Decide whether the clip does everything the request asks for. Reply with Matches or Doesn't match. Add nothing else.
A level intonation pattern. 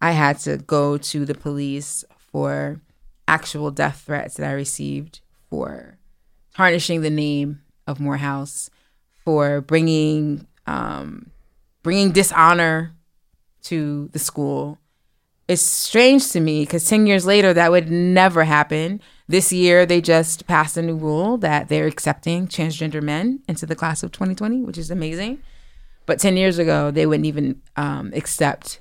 Doesn't match